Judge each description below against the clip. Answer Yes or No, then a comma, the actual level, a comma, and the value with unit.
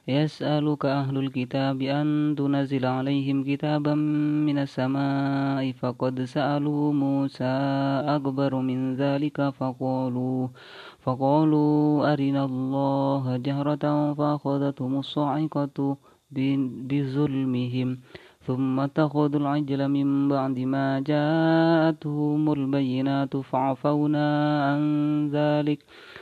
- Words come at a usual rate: No, slow, 80 wpm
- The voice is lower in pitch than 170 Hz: Yes, medium, 140 Hz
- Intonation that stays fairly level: Yes, narrow, 1.7 semitones